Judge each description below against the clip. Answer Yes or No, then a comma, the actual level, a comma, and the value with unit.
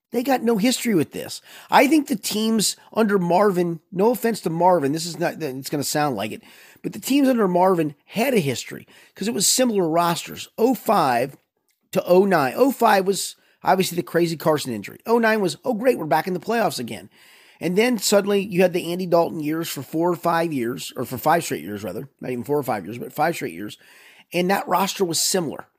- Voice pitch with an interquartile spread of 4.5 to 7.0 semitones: Yes, average, 5.1 semitones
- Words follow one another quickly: Yes, fast, 215 wpm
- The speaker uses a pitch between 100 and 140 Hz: No, medium, 185 Hz